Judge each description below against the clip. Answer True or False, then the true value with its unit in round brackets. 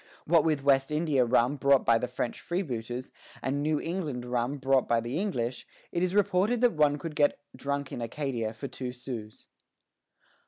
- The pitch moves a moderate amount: True (3.9 semitones)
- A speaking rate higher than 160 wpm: True (180 wpm)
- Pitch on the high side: False (140 Hz)